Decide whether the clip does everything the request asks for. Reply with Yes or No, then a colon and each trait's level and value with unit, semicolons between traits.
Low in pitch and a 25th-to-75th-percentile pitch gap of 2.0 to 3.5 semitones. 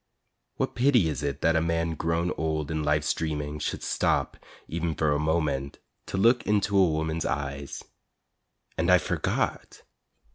Yes: very low, 80 Hz; narrow, 2.4 semitones